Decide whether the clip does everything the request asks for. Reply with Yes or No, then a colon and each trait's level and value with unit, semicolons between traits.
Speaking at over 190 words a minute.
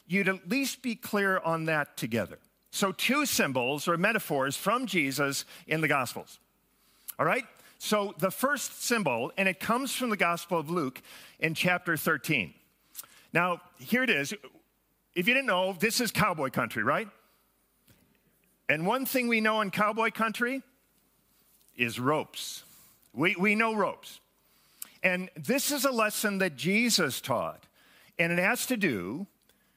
No: average, 150 wpm